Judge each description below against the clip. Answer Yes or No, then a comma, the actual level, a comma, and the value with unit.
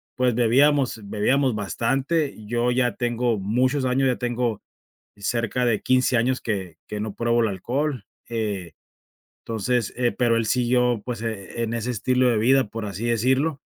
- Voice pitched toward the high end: No, low, 120 Hz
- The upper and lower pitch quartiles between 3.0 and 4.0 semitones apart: No, narrow, 2.5 semitones